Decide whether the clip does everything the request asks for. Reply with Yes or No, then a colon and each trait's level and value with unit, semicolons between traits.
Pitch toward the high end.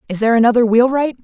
Yes: high, 240 Hz